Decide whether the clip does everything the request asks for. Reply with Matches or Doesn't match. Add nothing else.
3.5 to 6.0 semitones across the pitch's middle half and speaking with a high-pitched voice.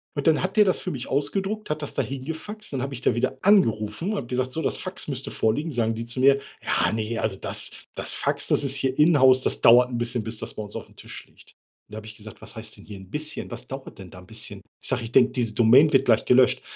Doesn't match